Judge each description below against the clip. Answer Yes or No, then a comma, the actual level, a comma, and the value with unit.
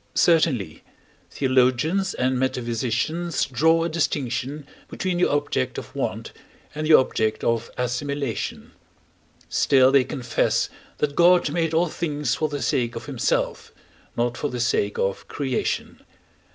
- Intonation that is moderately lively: Yes, average, 4.3 semitones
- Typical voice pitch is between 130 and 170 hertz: Yes, low, 135 Hz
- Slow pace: Yes, slow, 130 wpm